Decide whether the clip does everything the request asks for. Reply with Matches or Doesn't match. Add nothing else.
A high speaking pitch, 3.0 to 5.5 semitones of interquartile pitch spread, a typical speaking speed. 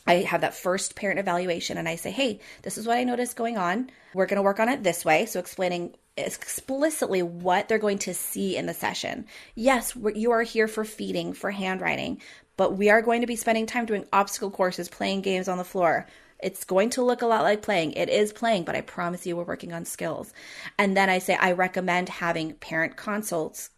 Doesn't match